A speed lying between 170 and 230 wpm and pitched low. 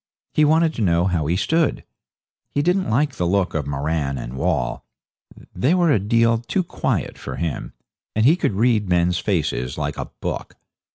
Yes: average, 180 wpm; low, 100 Hz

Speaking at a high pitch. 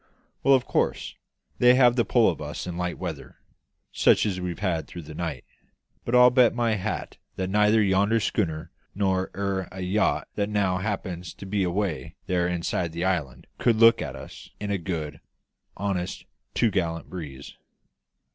No: very low, 95 Hz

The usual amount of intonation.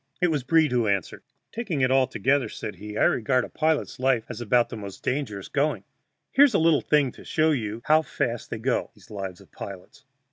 No: wide, 5.7 semitones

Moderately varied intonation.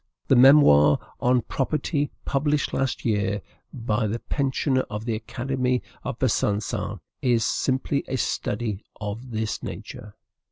Yes: average, 3.9 semitones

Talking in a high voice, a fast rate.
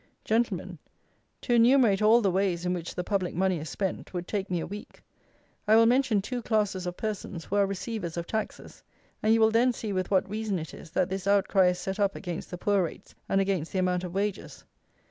Yes: high, 195 Hz; fast, 220 wpm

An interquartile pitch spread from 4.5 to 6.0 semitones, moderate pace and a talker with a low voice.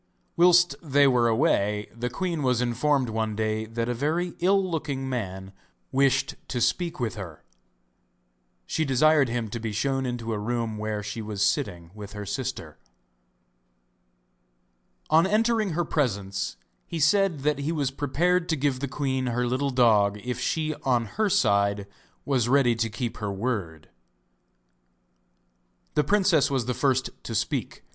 Yes: average, 5.3 semitones; average, 155 wpm; low, 125 Hz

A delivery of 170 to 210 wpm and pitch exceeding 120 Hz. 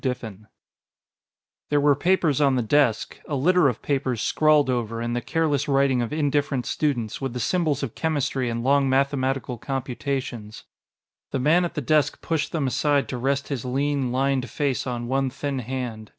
Yes: average, 175 wpm; low, 135 Hz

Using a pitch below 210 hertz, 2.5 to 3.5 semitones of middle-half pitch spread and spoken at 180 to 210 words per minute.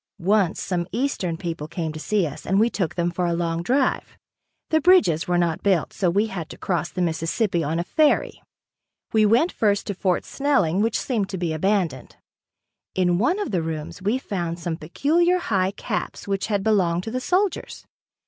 No: high, 190 Hz; average, 4.6 semitones; average, 195 wpm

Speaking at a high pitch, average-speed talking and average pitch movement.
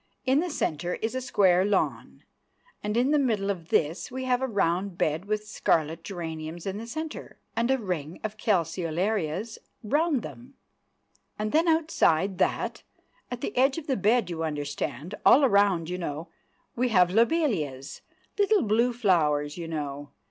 No: high, 200 Hz; average, 165 wpm; wide, 7.0 semitones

